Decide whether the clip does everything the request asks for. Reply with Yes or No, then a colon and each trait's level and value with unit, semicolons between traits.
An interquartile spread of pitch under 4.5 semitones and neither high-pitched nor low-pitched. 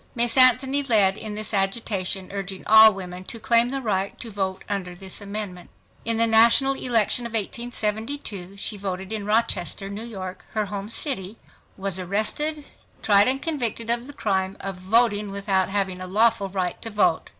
No: average, 3.2 semitones; high, 210 Hz